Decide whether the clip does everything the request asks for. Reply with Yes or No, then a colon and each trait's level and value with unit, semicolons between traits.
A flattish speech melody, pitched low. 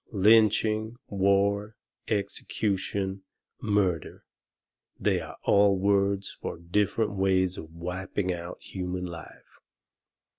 Yes: narrow, 1.9 semitones; low, 100 Hz